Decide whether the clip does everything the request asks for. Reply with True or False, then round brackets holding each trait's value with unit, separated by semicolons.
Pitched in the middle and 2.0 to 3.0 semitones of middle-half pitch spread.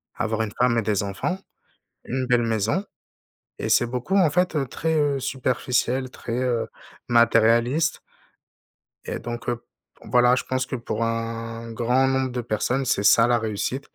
False (120 Hz; 2.5 semitones)